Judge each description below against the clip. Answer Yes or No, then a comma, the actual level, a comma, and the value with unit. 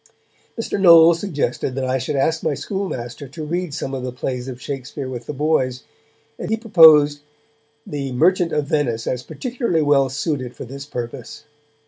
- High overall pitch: No, medium, 145 Hz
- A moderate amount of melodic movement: Yes, average, 4.0 semitones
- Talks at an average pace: Yes, average, 170 wpm